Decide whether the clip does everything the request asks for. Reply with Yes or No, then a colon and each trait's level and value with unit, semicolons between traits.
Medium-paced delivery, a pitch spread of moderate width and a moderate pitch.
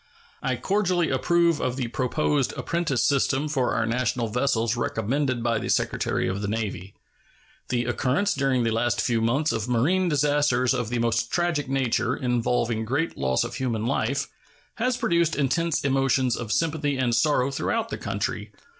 No: average, 165 wpm; average, 3.9 semitones; low, 130 Hz